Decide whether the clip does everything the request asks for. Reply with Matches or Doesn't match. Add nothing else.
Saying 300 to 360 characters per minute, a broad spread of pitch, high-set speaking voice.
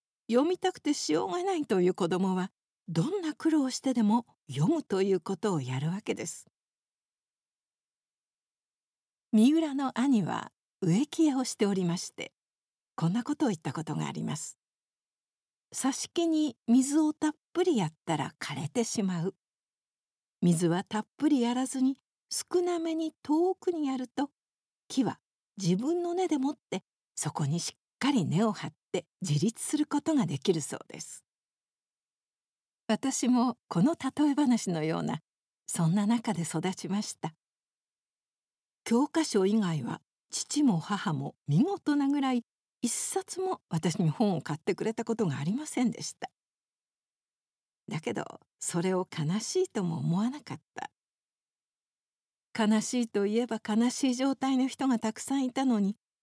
Doesn't match